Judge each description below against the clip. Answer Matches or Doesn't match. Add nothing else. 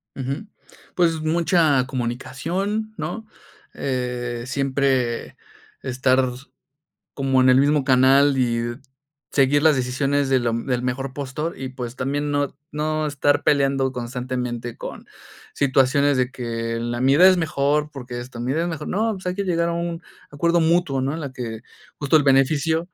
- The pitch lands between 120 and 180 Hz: Matches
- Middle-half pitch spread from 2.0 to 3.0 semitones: Doesn't match